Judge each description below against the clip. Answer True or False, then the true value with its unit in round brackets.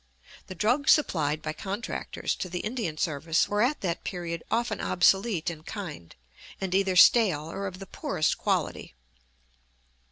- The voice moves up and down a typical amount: True (4.4 semitones)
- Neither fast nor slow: True (150 wpm)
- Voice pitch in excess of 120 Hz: True (185 Hz)